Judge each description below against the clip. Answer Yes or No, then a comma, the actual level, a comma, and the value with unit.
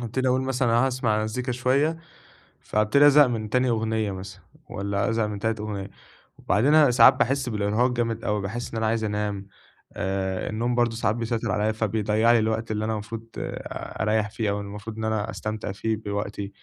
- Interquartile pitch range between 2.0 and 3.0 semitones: Yes, narrow, 2.4 semitones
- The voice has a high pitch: No, low, 110 Hz